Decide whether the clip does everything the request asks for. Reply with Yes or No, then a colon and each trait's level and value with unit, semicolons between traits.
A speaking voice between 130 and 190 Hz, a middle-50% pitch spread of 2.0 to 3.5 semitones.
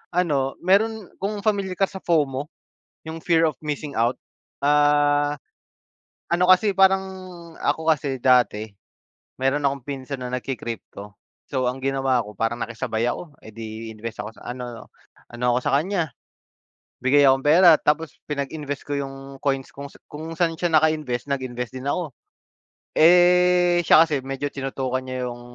No: medium, 140 Hz; average, 4.2 semitones